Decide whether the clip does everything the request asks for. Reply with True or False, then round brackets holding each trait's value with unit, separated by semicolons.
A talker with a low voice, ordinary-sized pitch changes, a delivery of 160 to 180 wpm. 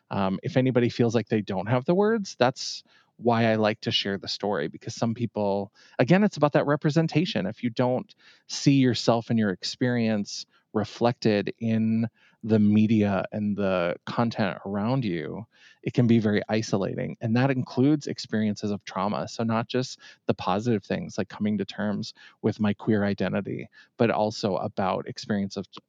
True (115 Hz; 3.2 semitones; 170 wpm)